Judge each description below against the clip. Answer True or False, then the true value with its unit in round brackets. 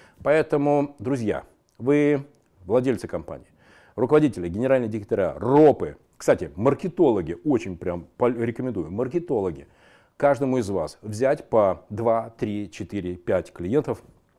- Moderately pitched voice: False (120 Hz)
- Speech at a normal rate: False (105 wpm)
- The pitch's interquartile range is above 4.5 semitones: True (5.3 semitones)